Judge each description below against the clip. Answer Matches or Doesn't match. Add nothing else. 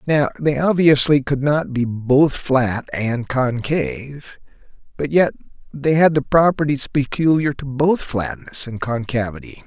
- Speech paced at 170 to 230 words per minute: Doesn't match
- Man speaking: Matches